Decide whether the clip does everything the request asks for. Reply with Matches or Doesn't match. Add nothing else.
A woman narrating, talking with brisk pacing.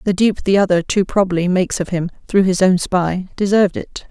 Matches